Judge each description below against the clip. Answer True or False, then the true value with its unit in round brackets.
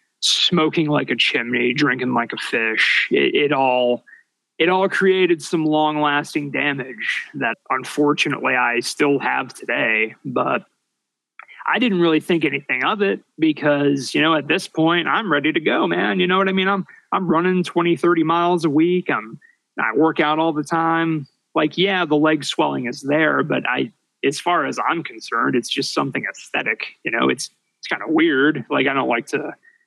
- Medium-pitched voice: True (160 Hz)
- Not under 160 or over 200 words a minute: True (185 wpm)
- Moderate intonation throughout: True (3.6 semitones)